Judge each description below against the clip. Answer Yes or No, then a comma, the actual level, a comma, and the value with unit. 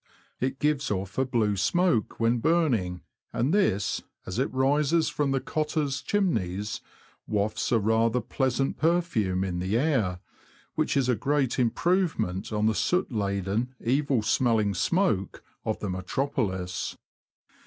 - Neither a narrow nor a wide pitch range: No, wide, 6.2 semitones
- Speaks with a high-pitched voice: No, low, 120 Hz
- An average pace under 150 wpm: Yes, slow, 135 wpm